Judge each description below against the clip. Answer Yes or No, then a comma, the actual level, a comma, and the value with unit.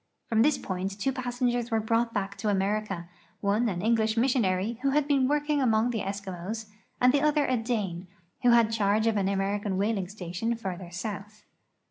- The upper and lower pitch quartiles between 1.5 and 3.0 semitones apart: No, average, 3.6 semitones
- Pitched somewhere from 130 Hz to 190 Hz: No, high, 220 Hz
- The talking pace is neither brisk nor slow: Yes, average, 185 wpm